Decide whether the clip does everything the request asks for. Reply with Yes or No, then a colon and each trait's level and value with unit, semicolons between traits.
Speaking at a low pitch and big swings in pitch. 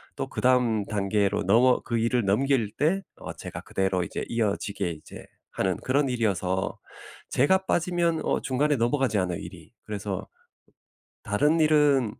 Yes: low, 115 Hz; wide, 5.9 semitones